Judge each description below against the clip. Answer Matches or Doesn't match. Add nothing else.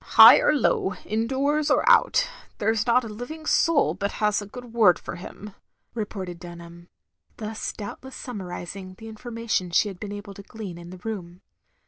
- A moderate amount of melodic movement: Matches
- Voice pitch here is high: Matches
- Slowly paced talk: Doesn't match